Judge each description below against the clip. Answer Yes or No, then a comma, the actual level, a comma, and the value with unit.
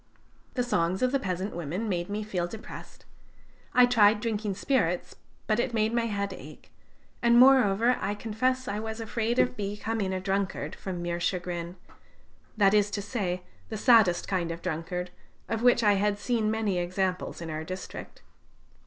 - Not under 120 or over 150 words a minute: No, average, 170 wpm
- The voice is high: Yes, high, 205 Hz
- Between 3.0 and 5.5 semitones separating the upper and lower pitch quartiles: Yes, average, 3.8 semitones